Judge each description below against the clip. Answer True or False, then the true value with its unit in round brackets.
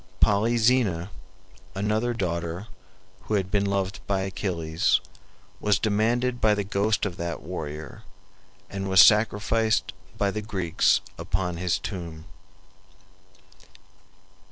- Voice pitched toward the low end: True (100 Hz)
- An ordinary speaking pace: False (105 wpm)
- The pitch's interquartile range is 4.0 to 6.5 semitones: False (3.2 semitones)